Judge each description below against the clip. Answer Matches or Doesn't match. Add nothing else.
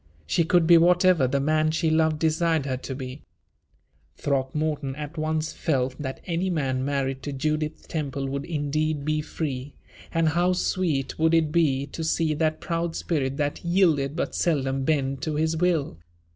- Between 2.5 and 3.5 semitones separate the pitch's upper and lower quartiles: Matches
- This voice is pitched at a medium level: Matches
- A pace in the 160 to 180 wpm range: Matches